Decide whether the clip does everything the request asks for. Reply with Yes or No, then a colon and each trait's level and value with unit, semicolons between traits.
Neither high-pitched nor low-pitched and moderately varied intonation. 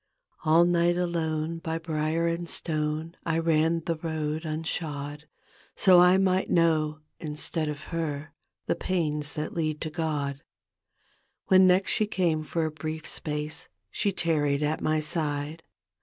No: medium, 160 Hz; narrow, 1.7 semitones